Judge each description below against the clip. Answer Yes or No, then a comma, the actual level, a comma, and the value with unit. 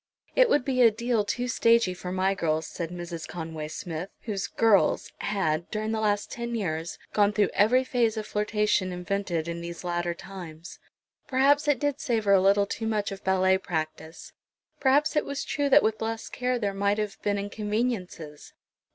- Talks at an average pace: Yes, average, 180 wpm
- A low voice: No, high, 205 Hz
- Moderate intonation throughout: Yes, average, 4.6 semitones